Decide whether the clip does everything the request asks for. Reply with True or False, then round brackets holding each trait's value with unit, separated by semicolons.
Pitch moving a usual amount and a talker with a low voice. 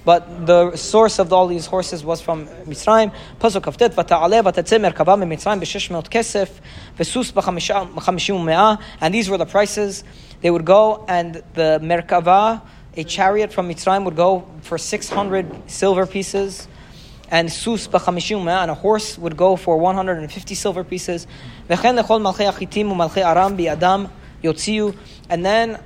False (3.2 semitones; 185 Hz)